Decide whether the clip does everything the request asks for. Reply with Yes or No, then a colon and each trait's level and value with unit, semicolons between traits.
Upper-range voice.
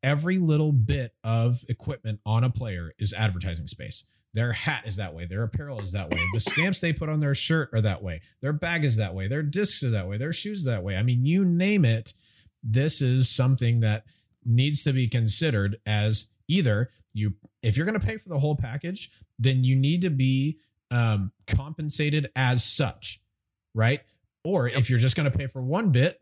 No: low, 125 Hz